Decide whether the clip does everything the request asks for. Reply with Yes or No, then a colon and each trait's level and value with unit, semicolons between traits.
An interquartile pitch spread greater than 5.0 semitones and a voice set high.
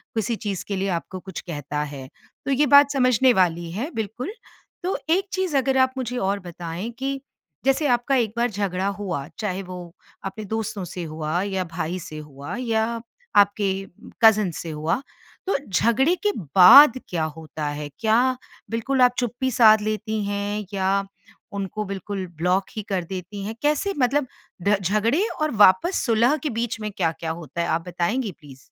Yes: wide, 5.4 semitones; high, 205 Hz